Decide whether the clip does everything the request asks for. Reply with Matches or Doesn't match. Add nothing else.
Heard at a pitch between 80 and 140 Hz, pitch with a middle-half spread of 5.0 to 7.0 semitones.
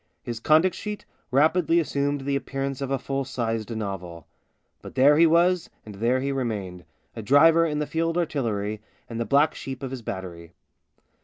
Matches